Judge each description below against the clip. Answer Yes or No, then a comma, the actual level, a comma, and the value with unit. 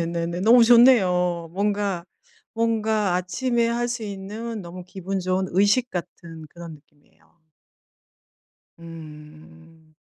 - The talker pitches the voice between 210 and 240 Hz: No, medium, 185 Hz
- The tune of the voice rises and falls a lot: No, average, 4.7 semitones